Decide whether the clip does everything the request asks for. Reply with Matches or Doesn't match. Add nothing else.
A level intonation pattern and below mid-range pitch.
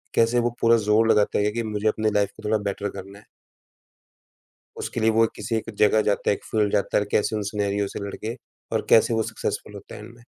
Matches